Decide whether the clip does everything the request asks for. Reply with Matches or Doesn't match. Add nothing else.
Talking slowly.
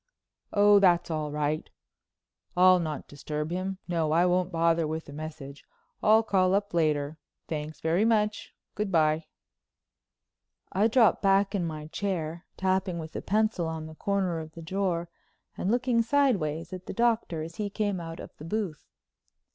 Doesn't match